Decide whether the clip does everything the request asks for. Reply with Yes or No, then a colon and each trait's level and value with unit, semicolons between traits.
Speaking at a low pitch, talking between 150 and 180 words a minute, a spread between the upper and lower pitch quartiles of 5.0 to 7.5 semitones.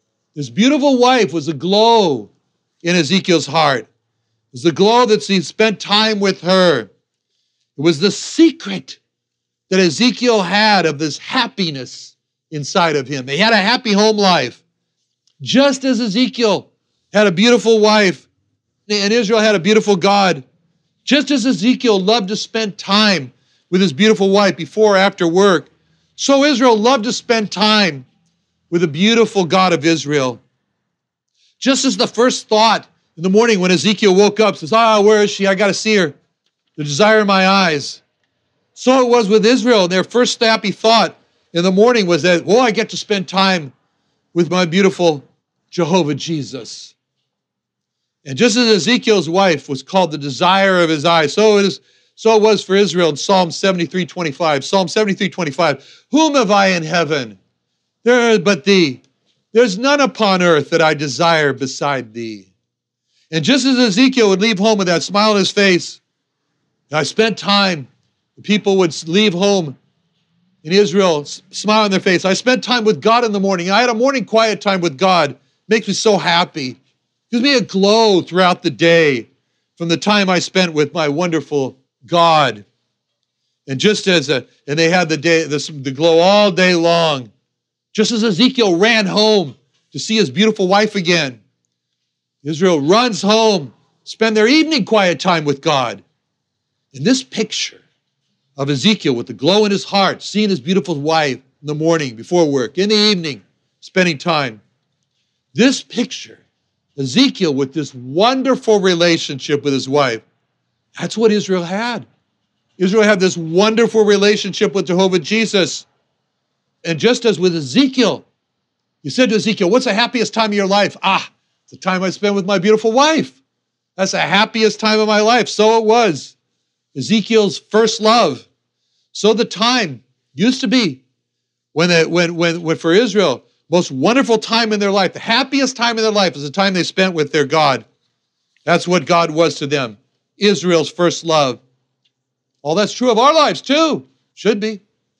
No: high, 190 Hz; average, 170 wpm; wide, 5.4 semitones